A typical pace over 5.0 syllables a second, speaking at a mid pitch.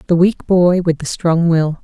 No: 4.4 syllables/s; medium, 170 Hz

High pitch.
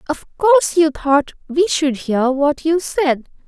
Yes: very high, 305 Hz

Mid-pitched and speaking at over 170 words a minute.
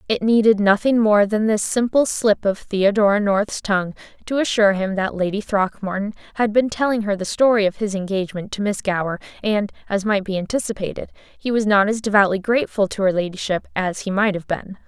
No: high, 205 Hz; average, 200 wpm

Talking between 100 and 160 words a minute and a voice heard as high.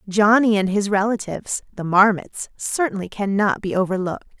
Yes: slow, 135 wpm; high, 200 Hz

